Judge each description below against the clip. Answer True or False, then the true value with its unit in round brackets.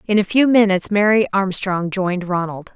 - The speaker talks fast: False (175 wpm)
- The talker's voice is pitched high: True (195 Hz)